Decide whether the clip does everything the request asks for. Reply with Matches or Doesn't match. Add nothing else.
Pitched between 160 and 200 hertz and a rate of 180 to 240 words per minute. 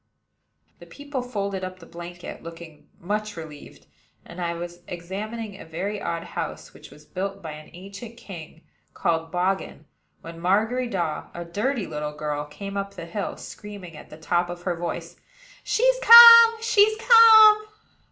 Doesn't match